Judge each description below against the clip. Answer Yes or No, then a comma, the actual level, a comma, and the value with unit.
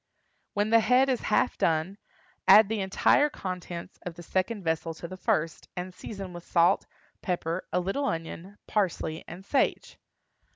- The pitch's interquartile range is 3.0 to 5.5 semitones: Yes, average, 3.5 semitones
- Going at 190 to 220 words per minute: No, average, 160 wpm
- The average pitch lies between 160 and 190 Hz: Yes, medium, 185 Hz